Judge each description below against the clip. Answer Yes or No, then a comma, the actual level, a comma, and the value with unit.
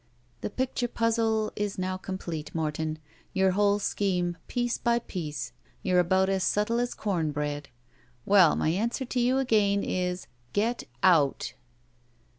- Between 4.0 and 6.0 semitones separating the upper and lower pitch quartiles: Yes, average, 4.6 semitones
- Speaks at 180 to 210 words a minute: No, average, 140 wpm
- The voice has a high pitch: Yes, high, 195 Hz